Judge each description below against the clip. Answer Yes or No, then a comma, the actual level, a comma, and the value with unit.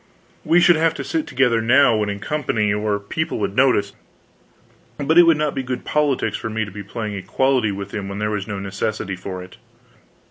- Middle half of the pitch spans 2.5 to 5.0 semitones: No, wide, 5.5 semitones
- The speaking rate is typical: No, fast, 210 wpm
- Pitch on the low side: Yes, low, 110 Hz